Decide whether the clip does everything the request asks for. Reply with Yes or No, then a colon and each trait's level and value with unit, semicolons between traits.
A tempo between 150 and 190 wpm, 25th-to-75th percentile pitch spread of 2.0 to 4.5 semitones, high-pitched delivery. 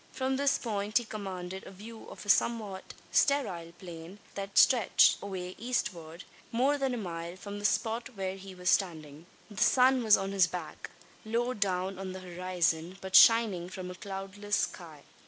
Yes: average, 175 wpm; average, 3.6 semitones; high, 195 Hz